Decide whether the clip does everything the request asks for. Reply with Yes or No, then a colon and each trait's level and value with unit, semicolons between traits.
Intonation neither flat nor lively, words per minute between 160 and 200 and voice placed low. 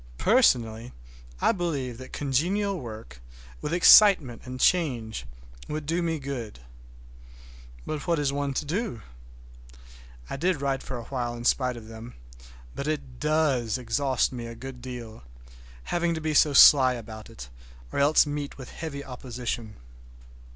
No: average, 4.6 semitones; average, 145 wpm; low, 130 Hz